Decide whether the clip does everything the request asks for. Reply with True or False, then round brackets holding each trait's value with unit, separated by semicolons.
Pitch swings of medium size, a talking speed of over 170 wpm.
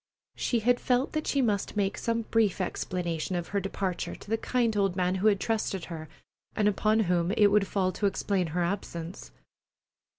True (3.4 semitones; 190 wpm)